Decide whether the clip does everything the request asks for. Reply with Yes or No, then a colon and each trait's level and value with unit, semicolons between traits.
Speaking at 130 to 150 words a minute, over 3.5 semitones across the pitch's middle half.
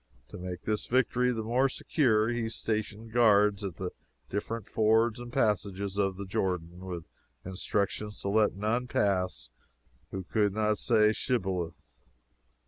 No: average, 140 wpm; average, 3.0 semitones